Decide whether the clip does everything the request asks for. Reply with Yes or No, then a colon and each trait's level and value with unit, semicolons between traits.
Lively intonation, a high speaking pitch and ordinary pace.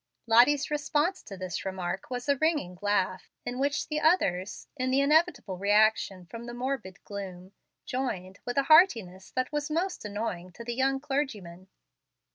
Yes: wide, 7.0 semitones; high, 240 Hz; average, 160 wpm